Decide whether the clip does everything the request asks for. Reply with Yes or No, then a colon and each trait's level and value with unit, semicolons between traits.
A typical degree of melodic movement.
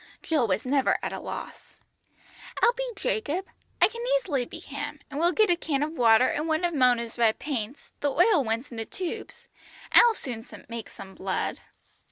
No: wide, 6.8 semitones